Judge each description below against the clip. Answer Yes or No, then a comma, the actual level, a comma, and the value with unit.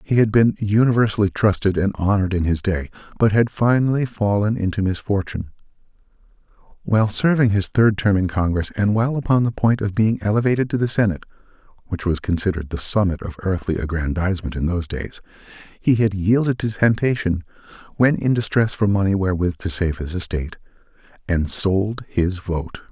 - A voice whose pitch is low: Yes, low, 100 Hz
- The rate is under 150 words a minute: No, average, 160 wpm